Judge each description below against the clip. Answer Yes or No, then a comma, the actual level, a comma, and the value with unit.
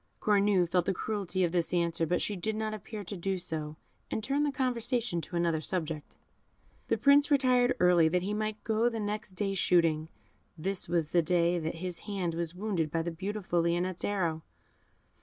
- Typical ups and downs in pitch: Yes, average, 4.0 semitones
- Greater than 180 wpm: Yes, average, 190 wpm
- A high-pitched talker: No, medium, 180 Hz